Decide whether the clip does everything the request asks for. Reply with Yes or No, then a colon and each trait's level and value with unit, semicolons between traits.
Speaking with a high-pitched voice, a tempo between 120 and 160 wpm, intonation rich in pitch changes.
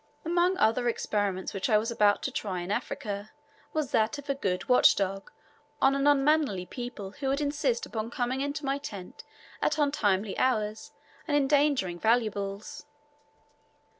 Yes: high, 235 Hz; average, 155 wpm; wide, 5.7 semitones